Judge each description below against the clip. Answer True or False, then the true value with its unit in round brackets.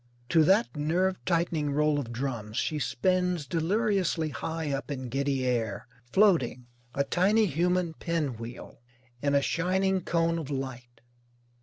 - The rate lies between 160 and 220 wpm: False (140 wpm)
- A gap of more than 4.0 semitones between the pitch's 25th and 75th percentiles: True (5.0 semitones)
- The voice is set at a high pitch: False (155 Hz)